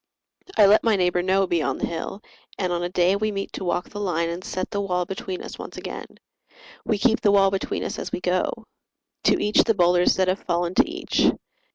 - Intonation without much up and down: Yes, narrow, 2.3 semitones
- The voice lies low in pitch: No, medium, 185 Hz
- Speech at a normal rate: No, fast, 225 wpm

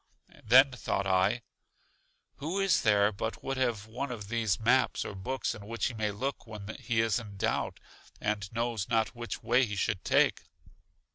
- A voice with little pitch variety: No, average, 3.0 semitones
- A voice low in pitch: Yes, low, 110 Hz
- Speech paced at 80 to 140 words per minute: No, average, 180 wpm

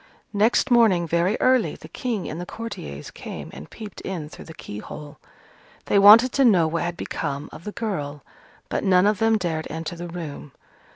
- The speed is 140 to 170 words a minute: No, average, 185 wpm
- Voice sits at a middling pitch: Yes, medium, 175 Hz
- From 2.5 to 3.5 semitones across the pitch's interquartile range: No, average, 5.3 semitones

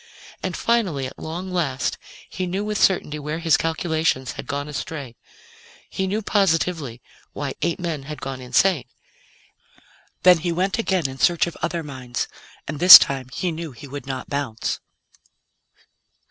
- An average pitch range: Yes, average, 4.7 semitones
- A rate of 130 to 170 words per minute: Yes, average, 155 wpm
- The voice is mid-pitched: Yes, medium, 160 Hz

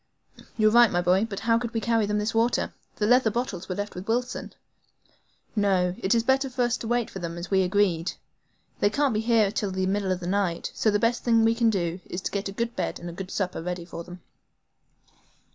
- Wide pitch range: No, average, 3.9 semitones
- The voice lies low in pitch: No, high, 205 Hz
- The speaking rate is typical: No, fast, 245 wpm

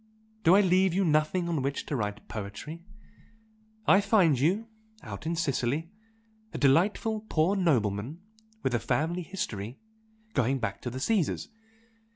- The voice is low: No, medium, 155 Hz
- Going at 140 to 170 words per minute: Yes, average, 145 wpm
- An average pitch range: No, wide, 6.6 semitones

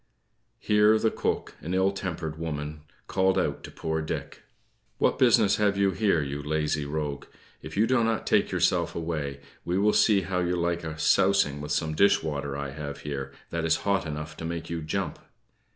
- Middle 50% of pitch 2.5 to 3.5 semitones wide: No, average, 4.6 semitones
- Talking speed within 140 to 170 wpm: No, average, 190 wpm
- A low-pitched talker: Yes, very low, 80 Hz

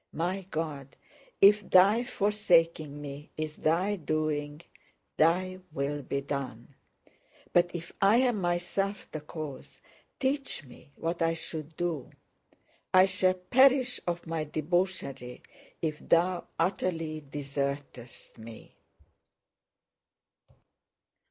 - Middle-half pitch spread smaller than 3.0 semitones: No, average, 4.1 semitones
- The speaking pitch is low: No, medium, 165 Hz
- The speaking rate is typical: No, slow, 105 wpm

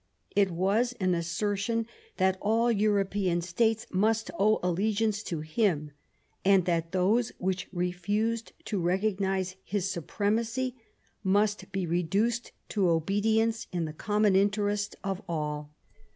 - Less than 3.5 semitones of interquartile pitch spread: Yes, average, 3.1 semitones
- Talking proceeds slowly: Yes, slow, 125 wpm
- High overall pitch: Yes, high, 200 Hz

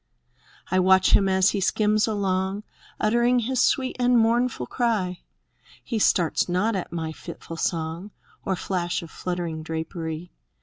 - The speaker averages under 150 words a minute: Yes, average, 140 wpm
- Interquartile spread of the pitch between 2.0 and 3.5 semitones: No, average, 4.2 semitones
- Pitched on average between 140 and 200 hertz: Yes, high, 190 Hz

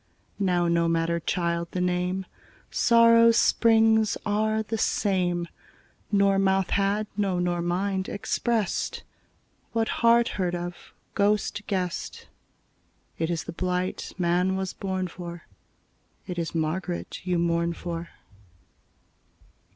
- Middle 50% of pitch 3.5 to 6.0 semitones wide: No, average, 2.9 semitones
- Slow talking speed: Yes, slow, 115 wpm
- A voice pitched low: No, medium, 185 Hz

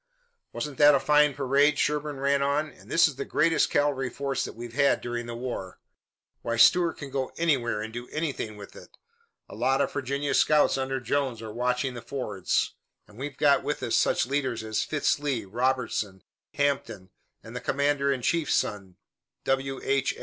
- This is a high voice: No, low, 135 Hz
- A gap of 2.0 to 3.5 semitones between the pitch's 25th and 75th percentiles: Yes, average, 3.2 semitones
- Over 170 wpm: Yes, average, 185 wpm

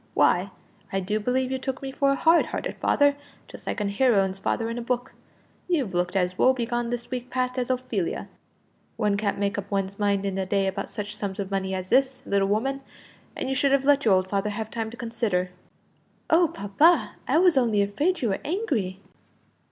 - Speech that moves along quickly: Yes, fast, 210 wpm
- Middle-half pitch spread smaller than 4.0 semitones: No, average, 4.9 semitones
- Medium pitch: No, high, 225 Hz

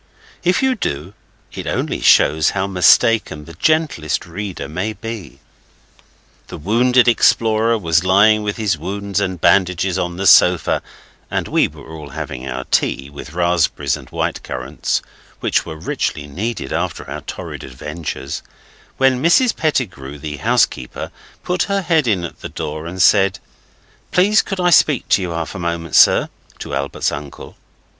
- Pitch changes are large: Yes, wide, 6.6 semitones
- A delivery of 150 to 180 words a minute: Yes, average, 155 wpm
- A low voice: Yes, very low, 95 Hz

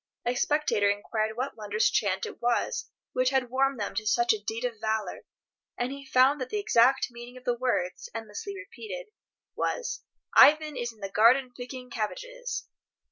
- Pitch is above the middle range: Yes, high, 245 Hz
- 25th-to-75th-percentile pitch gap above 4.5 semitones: No, average, 3.7 semitones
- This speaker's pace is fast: No, average, 175 wpm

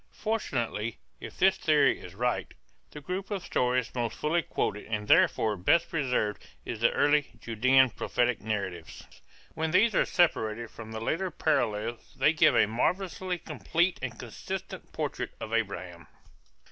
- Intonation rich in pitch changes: Yes, wide, 6.9 semitones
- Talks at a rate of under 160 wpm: Yes, average, 145 wpm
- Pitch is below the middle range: Yes, low, 125 Hz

